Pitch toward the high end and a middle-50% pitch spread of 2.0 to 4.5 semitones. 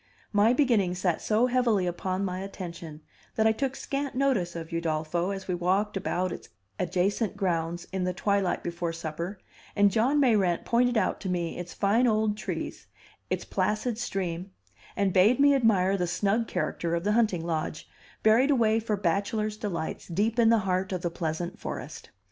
Yes: high, 195 Hz; average, 4.0 semitones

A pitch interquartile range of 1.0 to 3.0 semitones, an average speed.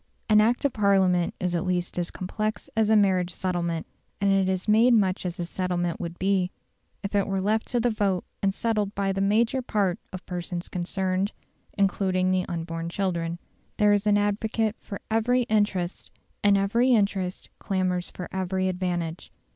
Yes: average, 2.7 semitones; average, 175 wpm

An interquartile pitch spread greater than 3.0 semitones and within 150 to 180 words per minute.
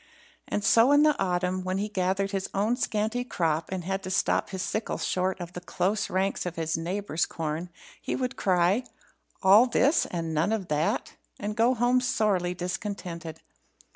Yes: average, 3.4 semitones; average, 175 wpm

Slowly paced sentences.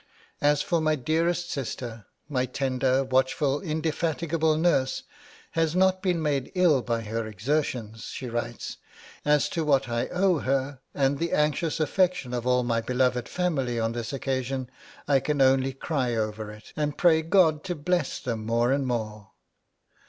No: average, 160 wpm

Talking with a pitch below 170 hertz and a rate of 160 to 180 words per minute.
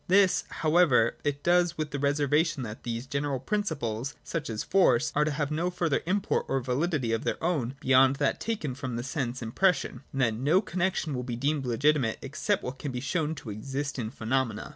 No: medium, 140 Hz; average, 200 wpm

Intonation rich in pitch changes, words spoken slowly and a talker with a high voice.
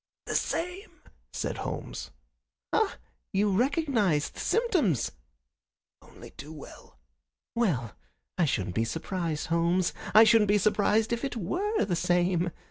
Yes: wide, 5.9 semitones; slow, 125 wpm; high, 195 Hz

